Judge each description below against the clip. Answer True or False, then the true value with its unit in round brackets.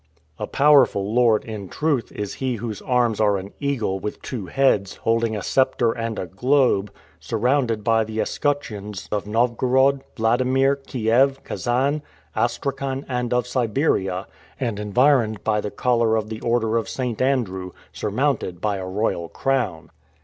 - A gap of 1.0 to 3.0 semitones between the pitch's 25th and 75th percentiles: False (3.8 semitones)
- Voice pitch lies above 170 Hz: False (115 Hz)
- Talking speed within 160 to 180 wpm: False (150 wpm)